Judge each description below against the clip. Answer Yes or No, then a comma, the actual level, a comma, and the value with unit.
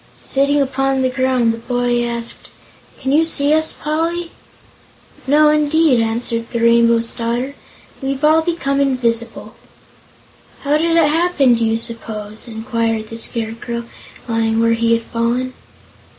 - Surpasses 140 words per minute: No, slow, 135 wpm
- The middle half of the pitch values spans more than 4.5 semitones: No, average, 3.8 semitones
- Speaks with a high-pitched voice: Yes, high, 245 Hz